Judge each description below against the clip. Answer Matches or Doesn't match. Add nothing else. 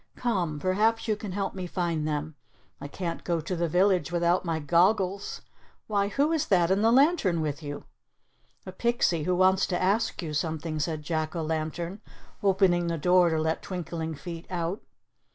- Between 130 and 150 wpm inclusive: Doesn't match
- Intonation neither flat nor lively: Matches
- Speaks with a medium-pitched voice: Matches